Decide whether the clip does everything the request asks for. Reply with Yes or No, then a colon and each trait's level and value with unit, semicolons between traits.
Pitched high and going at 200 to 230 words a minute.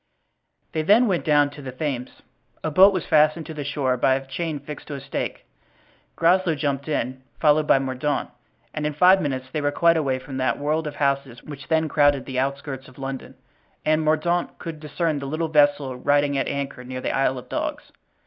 No: medium, 145 Hz; fast, 205 wpm